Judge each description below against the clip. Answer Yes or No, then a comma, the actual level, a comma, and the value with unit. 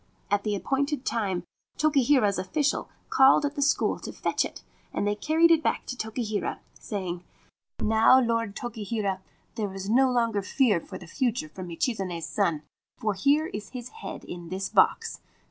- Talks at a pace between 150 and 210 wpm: Yes, average, 170 wpm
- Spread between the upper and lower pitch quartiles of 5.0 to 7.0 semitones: Yes, wide, 5.5 semitones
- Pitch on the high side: Yes, high, 220 Hz